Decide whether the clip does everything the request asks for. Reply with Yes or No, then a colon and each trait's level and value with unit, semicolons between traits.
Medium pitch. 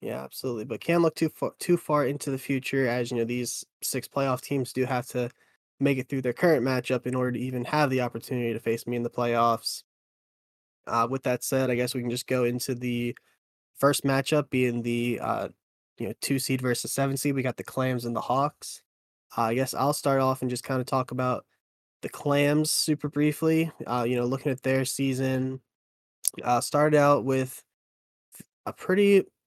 No: low, 130 Hz